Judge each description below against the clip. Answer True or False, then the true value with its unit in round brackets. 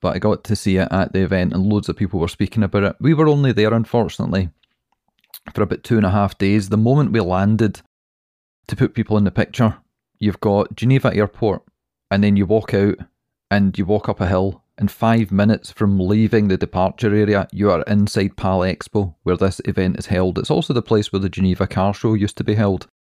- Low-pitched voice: True (100 Hz)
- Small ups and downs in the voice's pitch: True (2.2 semitones)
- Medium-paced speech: False (220 wpm)